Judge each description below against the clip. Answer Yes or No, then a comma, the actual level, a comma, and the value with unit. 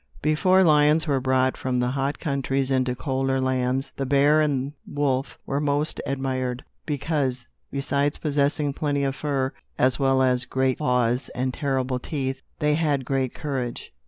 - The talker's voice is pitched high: No, low, 135 Hz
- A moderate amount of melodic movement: No, narrow, 1.9 semitones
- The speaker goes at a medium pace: Yes, average, 155 wpm